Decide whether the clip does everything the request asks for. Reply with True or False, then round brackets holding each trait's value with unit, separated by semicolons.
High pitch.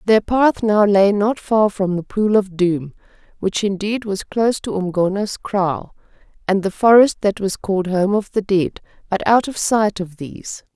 True (200 Hz)